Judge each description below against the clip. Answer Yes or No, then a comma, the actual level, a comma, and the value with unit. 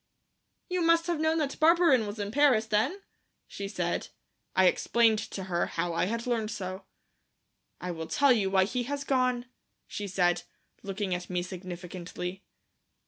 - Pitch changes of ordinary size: No, wide, 6.2 semitones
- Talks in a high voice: Yes, high, 210 Hz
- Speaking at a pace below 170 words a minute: Yes, average, 160 wpm